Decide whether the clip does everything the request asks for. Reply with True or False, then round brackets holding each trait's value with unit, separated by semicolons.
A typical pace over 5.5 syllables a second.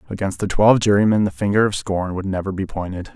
True (6.4 syllables/s)